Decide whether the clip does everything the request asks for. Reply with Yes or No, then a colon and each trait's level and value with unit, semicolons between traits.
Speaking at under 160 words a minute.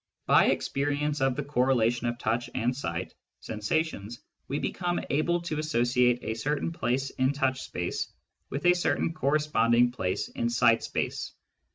Yes: average, 150 wpm